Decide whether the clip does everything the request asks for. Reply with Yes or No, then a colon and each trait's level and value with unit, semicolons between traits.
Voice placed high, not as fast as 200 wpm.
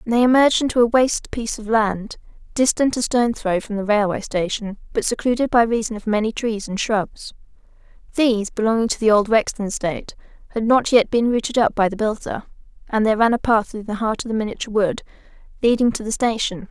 No: high, 220 Hz; fast, 205 wpm